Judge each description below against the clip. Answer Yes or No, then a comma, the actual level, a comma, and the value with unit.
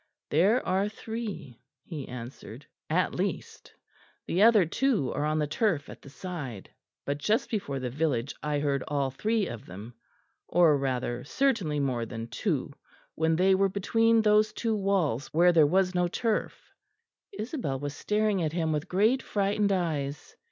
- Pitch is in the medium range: Yes, medium, 165 Hz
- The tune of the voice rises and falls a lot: Yes, wide, 6.9 semitones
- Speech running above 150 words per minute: Yes, average, 160 wpm